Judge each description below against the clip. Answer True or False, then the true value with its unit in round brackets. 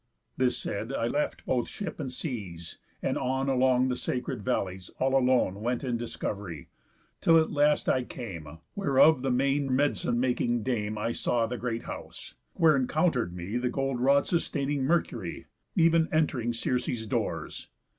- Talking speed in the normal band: True (160 wpm)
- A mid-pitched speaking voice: False (125 Hz)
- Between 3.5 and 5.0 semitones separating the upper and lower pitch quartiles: False (3.1 semitones)